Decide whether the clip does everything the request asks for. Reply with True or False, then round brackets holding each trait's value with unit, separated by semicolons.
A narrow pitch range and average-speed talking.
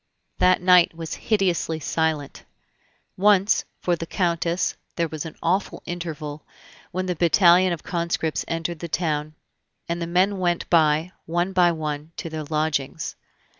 True (2.3 semitones; 145 wpm)